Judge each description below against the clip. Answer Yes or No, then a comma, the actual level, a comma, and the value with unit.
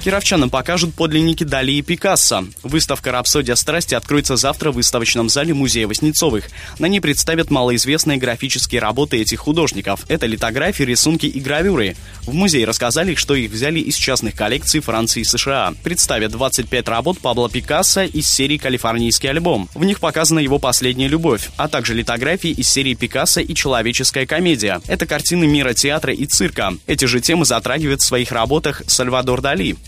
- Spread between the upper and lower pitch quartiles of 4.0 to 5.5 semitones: Yes, average, 4.4 semitones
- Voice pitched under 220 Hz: Yes, medium, 140 Hz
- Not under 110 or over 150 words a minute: No, fast, 160 wpm